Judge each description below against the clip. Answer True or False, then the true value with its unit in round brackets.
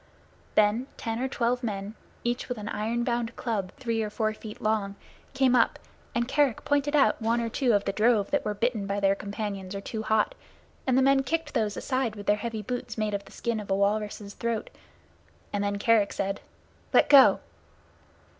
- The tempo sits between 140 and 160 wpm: False (200 wpm)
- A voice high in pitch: True (220 Hz)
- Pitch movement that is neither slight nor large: True (3.1 semitones)